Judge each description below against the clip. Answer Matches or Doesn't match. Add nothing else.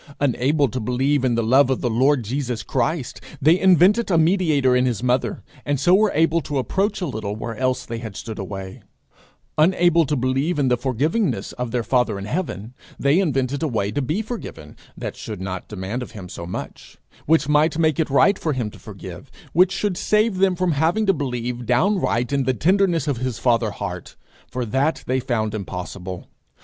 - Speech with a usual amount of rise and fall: Doesn't match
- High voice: Doesn't match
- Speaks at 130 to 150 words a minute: Doesn't match